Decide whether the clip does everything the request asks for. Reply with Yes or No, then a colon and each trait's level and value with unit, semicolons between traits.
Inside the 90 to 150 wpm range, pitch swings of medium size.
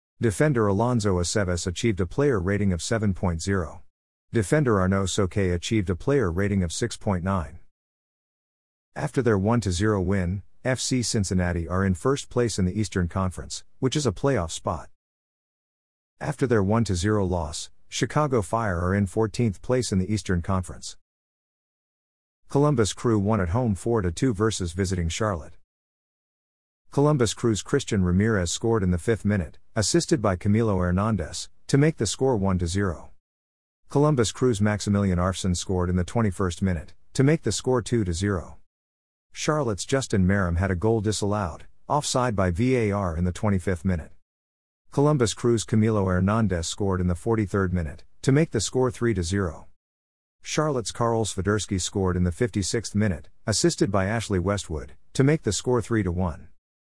Yes: average, 145 wpm; average, 4.4 semitones